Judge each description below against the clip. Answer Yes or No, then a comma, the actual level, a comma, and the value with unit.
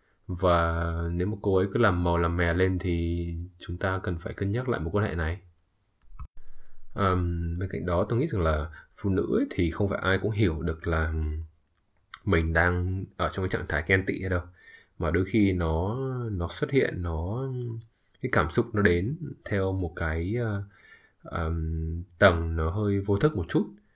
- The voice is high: No, very low, 90 Hz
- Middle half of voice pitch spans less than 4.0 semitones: Yes, average, 3.2 semitones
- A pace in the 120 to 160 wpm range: No, average, 195 wpm